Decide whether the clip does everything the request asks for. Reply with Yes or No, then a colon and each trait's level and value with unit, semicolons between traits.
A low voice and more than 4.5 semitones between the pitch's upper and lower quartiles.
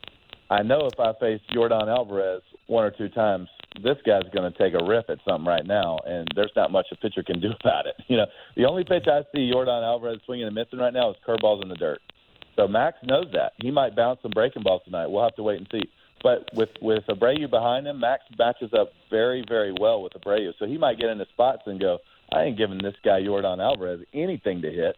Yes: low, 115 Hz; average, 5.2 semitones